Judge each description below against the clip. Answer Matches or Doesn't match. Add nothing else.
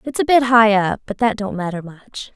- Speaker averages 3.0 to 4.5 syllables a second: Doesn't match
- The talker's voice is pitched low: Doesn't match